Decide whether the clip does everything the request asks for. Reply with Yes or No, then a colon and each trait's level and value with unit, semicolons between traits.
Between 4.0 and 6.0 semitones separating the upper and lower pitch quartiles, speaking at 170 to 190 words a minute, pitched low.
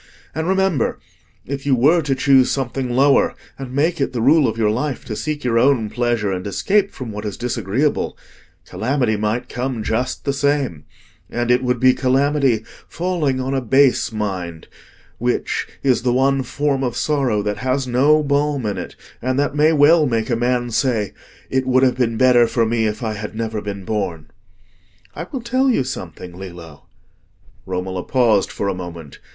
Yes: average, 4.4 semitones; average, 180 wpm; low, 125 Hz